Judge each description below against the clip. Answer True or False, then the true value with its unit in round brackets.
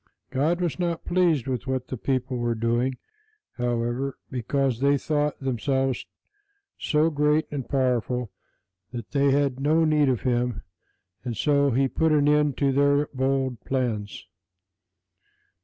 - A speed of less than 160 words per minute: True (140 wpm)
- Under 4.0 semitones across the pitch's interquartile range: True (2.9 semitones)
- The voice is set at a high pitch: False (135 Hz)